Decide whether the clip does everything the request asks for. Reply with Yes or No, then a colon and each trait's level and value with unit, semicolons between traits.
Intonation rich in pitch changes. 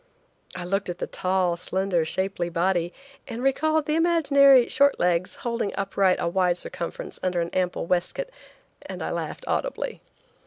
Yes: wide, 7.4 semitones